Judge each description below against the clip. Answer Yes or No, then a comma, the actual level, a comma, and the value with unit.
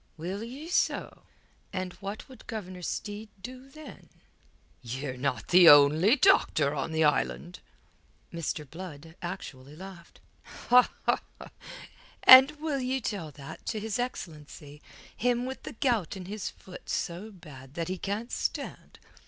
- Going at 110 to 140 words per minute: Yes, slow, 135 wpm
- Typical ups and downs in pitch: No, wide, 7.1 semitones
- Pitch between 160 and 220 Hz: Yes, medium, 185 Hz